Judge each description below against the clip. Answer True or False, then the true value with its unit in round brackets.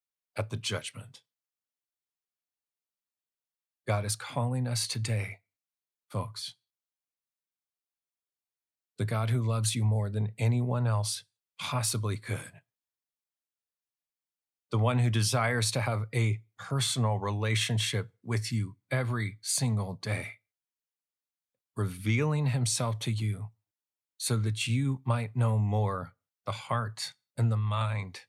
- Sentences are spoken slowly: True (105 wpm)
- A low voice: True (110 Hz)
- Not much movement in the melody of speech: True (2.1 semitones)